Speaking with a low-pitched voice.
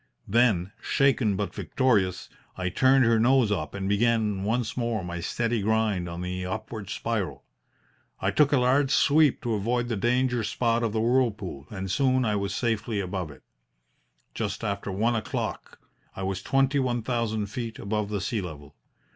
Yes: low, 110 Hz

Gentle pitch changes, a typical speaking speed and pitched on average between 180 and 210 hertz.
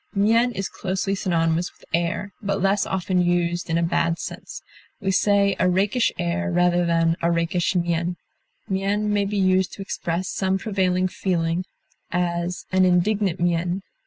Yes: narrow, 2.3 semitones; average, 160 wpm; medium, 185 Hz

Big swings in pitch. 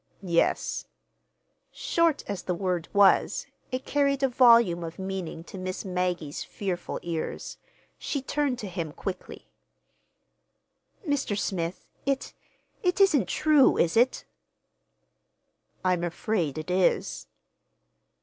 Yes: wide, 6.9 semitones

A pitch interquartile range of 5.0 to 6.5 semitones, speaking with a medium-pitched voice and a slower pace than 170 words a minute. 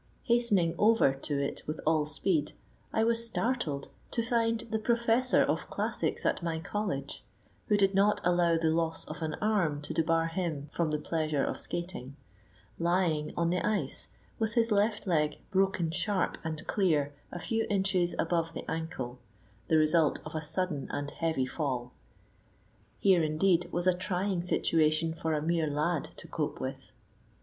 No: average, 4.2 semitones; medium, 170 Hz; average, 160 wpm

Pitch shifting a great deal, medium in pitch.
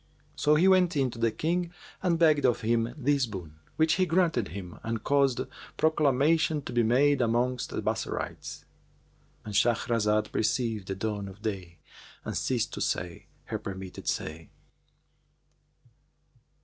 No: wide, 6.1 semitones; low, 120 Hz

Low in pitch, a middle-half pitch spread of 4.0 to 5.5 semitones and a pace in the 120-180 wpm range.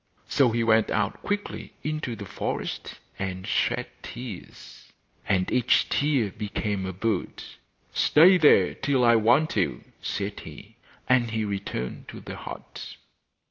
Yes: low, 110 Hz; average, 4.3 semitones; average, 140 wpm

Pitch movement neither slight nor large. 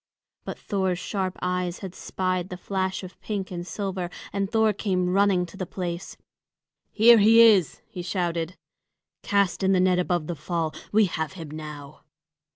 No: narrow, 2.1 semitones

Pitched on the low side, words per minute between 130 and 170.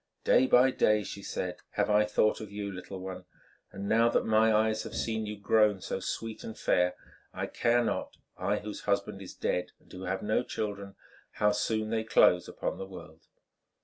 No: low, 105 Hz; average, 185 wpm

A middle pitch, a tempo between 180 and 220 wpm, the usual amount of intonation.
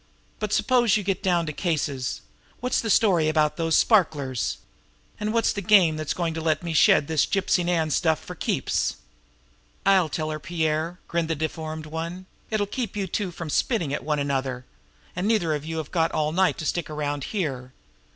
Yes: medium, 165 Hz; average, 190 wpm; average, 3.6 semitones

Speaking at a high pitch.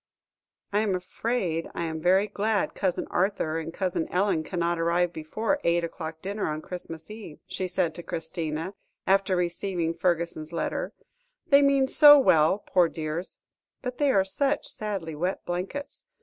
No: medium, 180 Hz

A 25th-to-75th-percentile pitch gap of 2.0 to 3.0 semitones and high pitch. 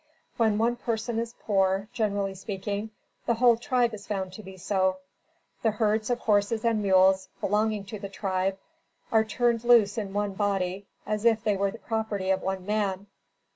Yes: narrow, 2.5 semitones; high, 205 Hz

